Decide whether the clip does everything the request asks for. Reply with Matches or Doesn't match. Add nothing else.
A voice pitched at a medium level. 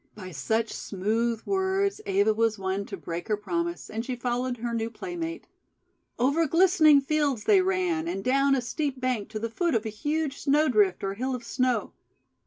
Doesn't match